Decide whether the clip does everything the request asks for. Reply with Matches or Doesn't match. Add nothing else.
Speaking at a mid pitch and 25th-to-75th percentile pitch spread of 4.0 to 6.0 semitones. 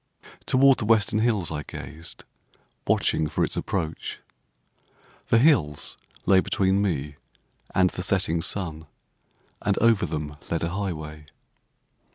Doesn't match